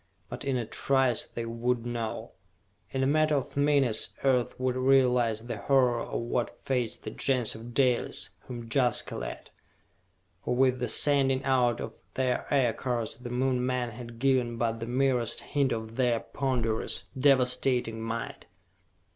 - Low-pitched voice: Yes, low, 125 Hz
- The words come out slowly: No, average, 155 wpm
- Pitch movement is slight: Yes, narrow, 2.2 semitones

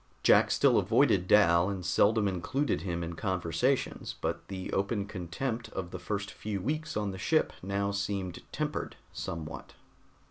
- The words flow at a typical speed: Yes, average, 150 wpm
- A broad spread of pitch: No, average, 3.0 semitones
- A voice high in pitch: No, low, 100 Hz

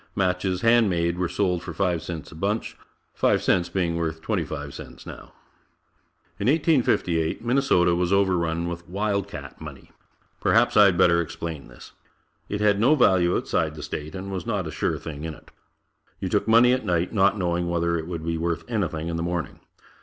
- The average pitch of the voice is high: No, very low, 90 Hz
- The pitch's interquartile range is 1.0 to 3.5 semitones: Yes, average, 3.1 semitones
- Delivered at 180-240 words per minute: Yes, average, 190 wpm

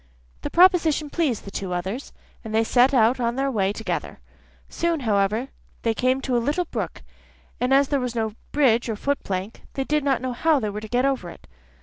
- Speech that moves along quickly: Yes, fast, 215 wpm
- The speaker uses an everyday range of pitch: Yes, average, 4.2 semitones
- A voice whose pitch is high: Yes, very high, 250 Hz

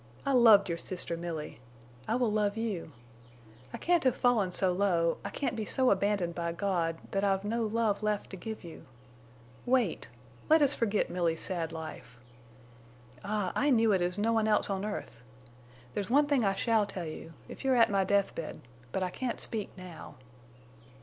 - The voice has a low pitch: No, high, 200 Hz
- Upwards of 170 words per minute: Yes, average, 180 wpm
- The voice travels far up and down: No, average, 4.3 semitones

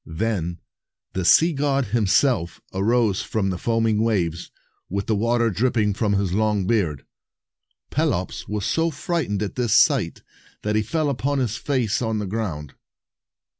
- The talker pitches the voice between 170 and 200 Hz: No, low, 110 Hz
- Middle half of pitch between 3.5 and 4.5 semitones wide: Yes, average, 3.8 semitones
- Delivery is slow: No, average, 150 wpm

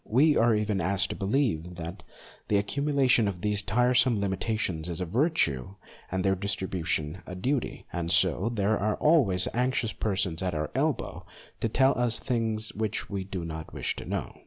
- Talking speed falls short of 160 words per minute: No, average, 180 wpm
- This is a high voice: No, low, 100 Hz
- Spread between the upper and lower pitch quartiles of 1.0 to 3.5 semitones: No, average, 4.5 semitones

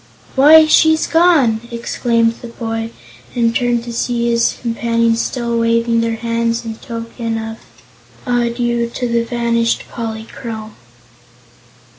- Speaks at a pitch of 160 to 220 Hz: No, high, 235 Hz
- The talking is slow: Yes, slow, 120 wpm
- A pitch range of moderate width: No, narrow, 0.7 semitones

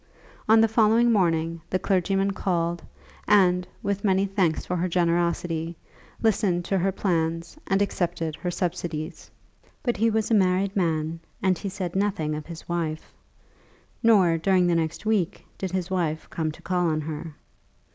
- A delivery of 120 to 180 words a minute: Yes, average, 160 wpm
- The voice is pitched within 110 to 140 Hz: No, medium, 180 Hz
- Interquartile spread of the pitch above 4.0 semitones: No, average, 2.9 semitones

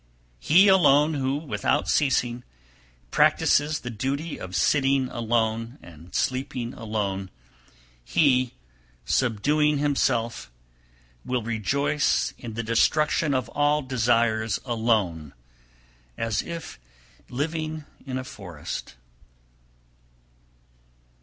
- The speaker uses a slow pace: Yes, slow, 95 wpm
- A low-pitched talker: Yes, low, 125 Hz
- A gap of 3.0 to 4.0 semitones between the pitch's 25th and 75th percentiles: No, average, 4.7 semitones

